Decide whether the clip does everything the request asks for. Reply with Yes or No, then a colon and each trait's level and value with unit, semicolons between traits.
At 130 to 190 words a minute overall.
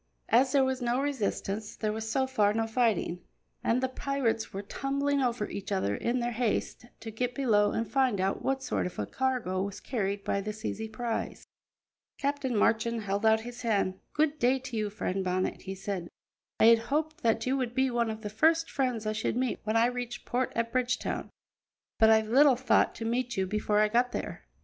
No: fast, 205 wpm